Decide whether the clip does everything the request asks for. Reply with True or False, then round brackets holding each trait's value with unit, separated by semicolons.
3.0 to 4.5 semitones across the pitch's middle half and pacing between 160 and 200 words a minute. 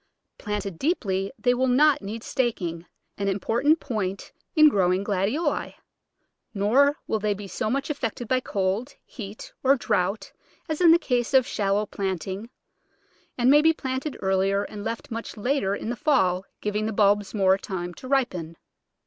False (5.0 semitones; 170 wpm)